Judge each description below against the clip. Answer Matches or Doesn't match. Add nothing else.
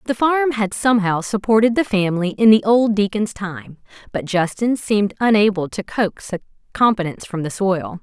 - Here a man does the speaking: Doesn't match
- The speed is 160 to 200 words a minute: Matches